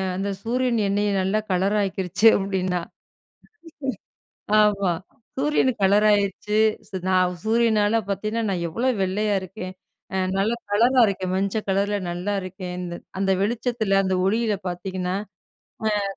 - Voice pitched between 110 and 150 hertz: No, high, 200 Hz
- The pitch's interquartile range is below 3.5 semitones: Yes, narrow, 2.6 semitones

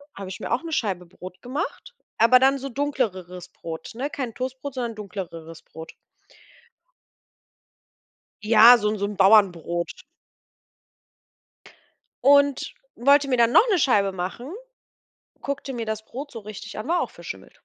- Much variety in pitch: Yes, wide, 6.0 semitones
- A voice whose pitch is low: No, high, 230 Hz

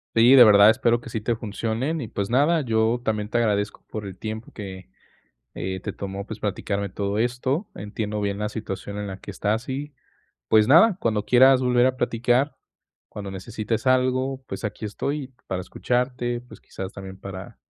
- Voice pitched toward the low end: Yes, low, 110 Hz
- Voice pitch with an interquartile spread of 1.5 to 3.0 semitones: No, average, 3.7 semitones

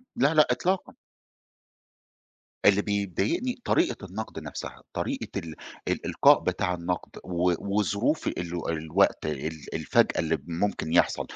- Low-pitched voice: Yes, very low, 90 Hz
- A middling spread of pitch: Yes, average, 4.0 semitones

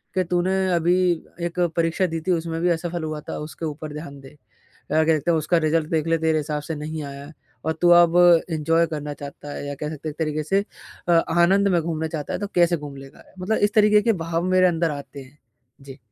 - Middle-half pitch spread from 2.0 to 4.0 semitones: Yes, narrow, 2.4 semitones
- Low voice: No, medium, 160 Hz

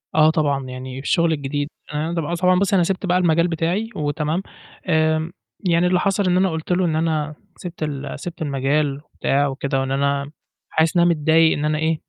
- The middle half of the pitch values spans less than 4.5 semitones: Yes, average, 3.1 semitones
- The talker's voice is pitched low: No, medium, 160 Hz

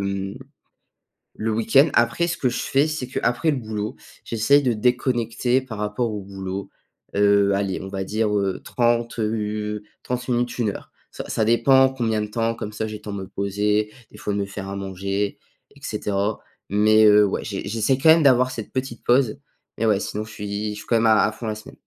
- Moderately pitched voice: No, low, 110 Hz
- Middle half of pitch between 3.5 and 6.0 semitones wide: No, average, 3.0 semitones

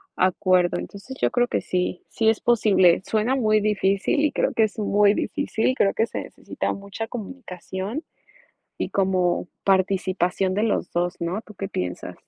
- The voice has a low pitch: No, high, 200 Hz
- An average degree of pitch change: Yes, average, 3.1 semitones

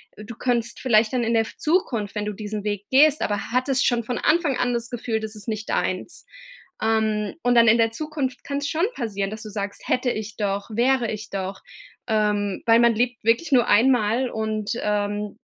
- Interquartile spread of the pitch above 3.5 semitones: No, average, 2.8 semitones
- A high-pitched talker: Yes, high, 225 Hz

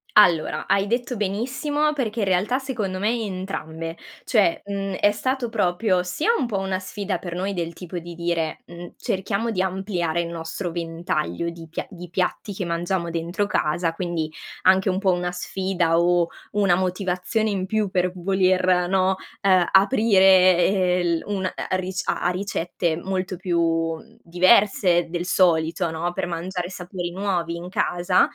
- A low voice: No, medium, 185 Hz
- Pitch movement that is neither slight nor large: No, narrow, 2.3 semitones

